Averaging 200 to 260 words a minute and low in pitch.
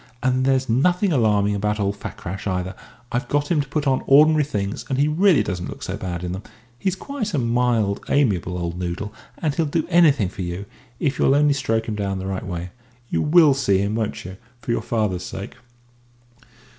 Yes: fast, 205 wpm; low, 115 Hz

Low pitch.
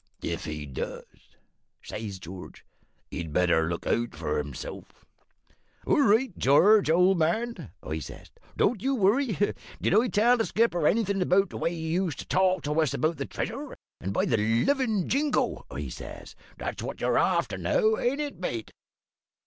No: medium, 180 Hz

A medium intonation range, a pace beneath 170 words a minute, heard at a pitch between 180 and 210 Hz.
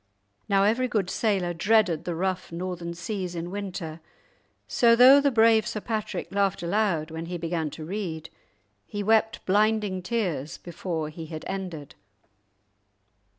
Yes: average, 4.1 semitones; average, 145 wpm; medium, 185 Hz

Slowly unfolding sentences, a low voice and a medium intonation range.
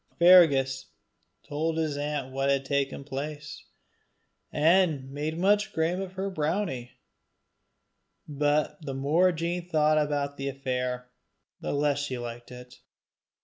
No: slow, 125 wpm; medium, 145 Hz; average, 3.2 semitones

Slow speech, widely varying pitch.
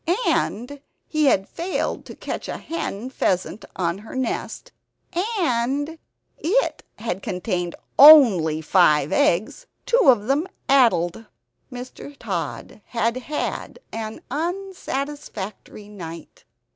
Yes: slow, 105 wpm; wide, 7.3 semitones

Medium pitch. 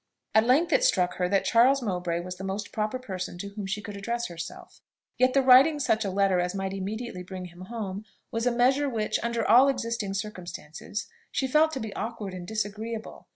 No: high, 215 Hz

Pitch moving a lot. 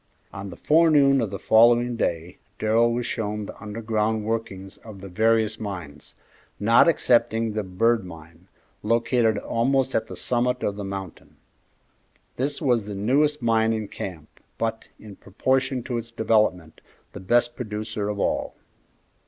No: average, 2.9 semitones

